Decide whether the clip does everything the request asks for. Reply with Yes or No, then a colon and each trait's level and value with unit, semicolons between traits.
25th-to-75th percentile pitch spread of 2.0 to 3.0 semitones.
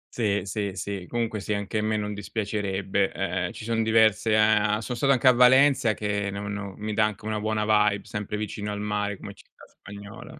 No: narrow, 1.4 semitones